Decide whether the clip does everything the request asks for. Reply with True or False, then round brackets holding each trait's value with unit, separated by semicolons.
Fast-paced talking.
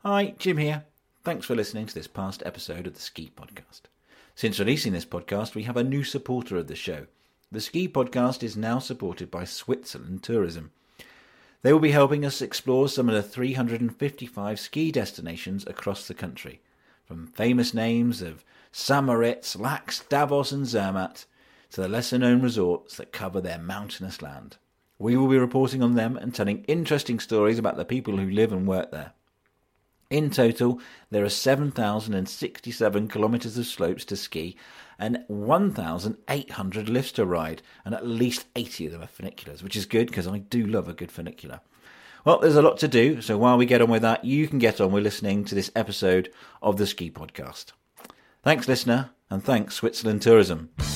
False (180 wpm)